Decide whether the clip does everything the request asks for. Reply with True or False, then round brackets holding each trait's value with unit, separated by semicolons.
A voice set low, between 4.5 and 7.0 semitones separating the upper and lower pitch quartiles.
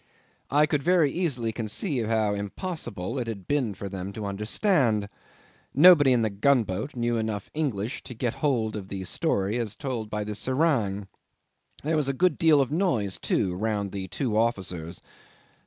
True (115 Hz; 5.6 semitones)